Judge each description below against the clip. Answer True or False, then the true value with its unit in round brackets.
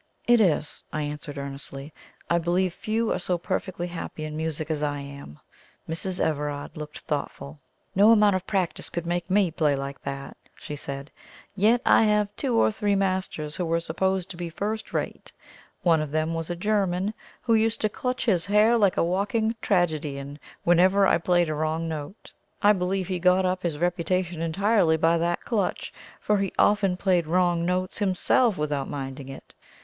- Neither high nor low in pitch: True (175 Hz)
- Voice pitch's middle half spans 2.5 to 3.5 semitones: False (4.2 semitones)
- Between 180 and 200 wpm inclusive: True (185 wpm)